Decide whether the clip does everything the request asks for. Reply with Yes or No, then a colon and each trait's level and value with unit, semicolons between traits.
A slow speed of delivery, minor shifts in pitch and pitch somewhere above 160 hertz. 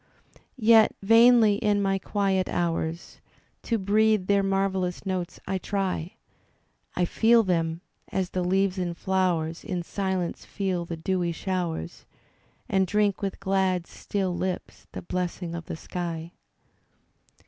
Yes: slow, 130 wpm; narrow, 2.2 semitones; high, 190 Hz